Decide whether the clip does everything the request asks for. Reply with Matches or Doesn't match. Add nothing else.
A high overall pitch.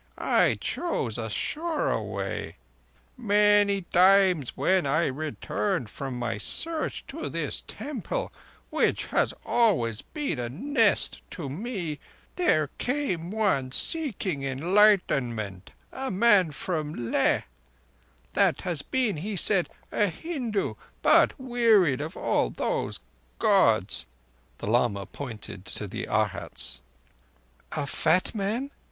Doesn't match